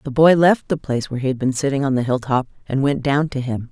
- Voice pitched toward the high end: No, low, 135 Hz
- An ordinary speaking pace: No, fast, 290 wpm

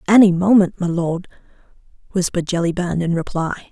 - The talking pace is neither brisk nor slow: No, slow, 130 wpm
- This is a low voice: No, medium, 180 Hz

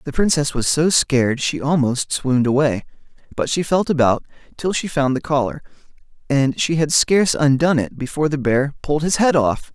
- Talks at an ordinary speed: Yes, average, 190 wpm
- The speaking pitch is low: No, medium, 145 Hz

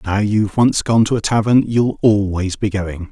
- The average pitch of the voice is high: No, low, 105 Hz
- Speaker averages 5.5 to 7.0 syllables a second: No, 4.8 syllables/s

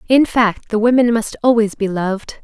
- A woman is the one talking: Yes, female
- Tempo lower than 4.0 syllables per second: No, 5.1 syllables/s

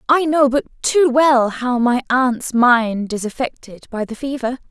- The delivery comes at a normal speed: Yes, average, 180 wpm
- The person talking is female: Yes, female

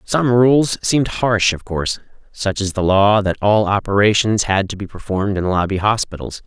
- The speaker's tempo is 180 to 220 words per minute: Yes, average, 185 wpm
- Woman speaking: No, male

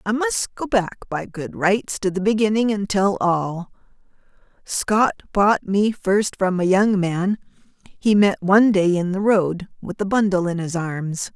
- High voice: Yes, high, 195 Hz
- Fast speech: No, average, 180 wpm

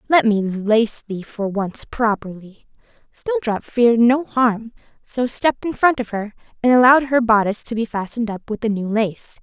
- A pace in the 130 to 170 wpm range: No, average, 185 wpm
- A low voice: No, high, 225 Hz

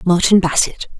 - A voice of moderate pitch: Yes, medium, 180 Hz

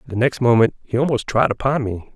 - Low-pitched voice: Yes, low, 120 Hz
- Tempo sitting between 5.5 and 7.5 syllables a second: Yes, 5.7 syllables/s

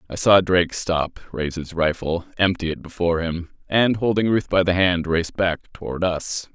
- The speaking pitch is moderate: No, very low, 90 Hz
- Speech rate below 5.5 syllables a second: Yes, 4.9 syllables/s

